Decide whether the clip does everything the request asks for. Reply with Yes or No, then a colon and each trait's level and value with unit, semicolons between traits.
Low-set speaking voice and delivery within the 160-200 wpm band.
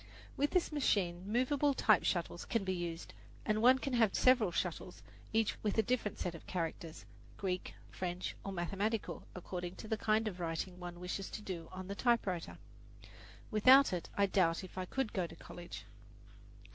No: high, 190 Hz; average, 175 wpm